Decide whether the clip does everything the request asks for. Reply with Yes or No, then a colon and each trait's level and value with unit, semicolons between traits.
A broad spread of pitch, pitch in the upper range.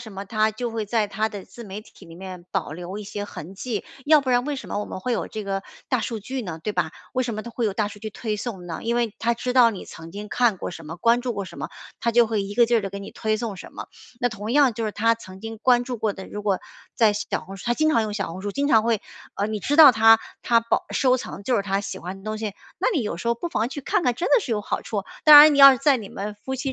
No: average, 3.4 semitones; high, 220 Hz